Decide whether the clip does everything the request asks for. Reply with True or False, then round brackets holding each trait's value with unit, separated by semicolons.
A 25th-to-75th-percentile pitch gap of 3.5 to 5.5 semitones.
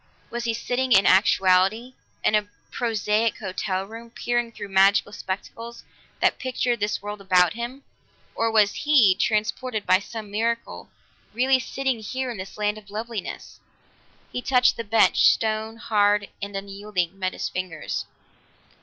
False (2.9 semitones)